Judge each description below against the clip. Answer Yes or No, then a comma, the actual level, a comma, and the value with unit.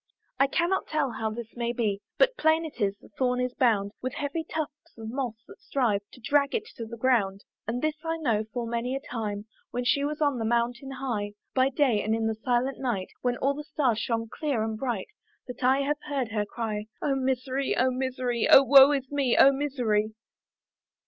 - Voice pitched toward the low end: No, very high, 250 Hz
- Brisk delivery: Yes, fast, 210 wpm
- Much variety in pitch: No, average, 3.6 semitones